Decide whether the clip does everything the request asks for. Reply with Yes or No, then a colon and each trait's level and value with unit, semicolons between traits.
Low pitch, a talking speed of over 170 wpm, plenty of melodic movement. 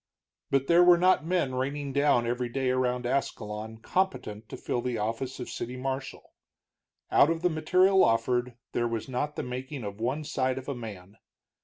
No: low, 130 Hz; average, 180 wpm; average, 3.6 semitones